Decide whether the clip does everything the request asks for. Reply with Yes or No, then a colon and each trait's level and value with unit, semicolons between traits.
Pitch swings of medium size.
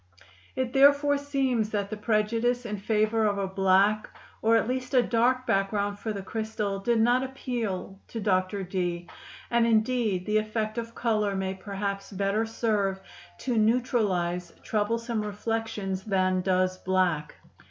Yes: average, 3.1 semitones